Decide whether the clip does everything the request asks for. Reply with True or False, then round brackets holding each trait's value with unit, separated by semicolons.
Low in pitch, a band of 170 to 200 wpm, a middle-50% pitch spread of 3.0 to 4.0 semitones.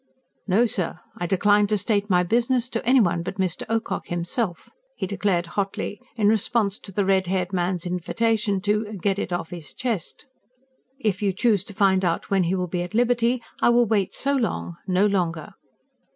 False (200 Hz; 185 wpm; 3.5 semitones)